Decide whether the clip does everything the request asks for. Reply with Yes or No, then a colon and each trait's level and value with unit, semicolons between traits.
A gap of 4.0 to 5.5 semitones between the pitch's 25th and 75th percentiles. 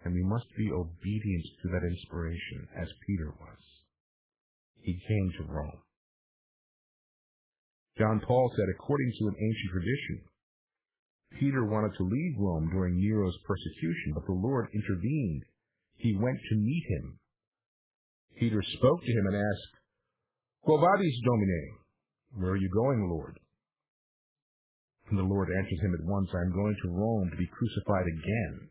No: average, 3.6 semitones